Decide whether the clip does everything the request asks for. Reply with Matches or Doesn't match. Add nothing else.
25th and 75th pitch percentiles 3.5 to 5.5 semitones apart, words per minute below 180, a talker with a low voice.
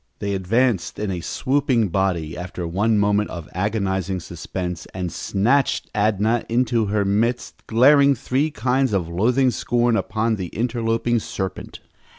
Matches